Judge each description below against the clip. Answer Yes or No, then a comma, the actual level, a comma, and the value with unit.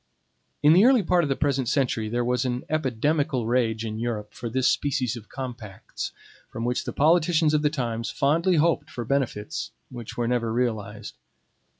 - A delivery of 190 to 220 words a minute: No, average, 180 wpm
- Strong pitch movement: No, average, 4.3 semitones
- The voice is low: Yes, low, 125 Hz